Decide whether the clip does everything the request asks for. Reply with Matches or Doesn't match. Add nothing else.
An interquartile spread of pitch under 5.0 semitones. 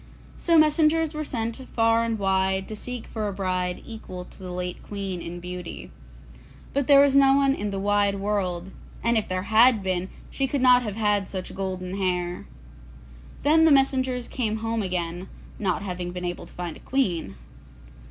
Doesn't match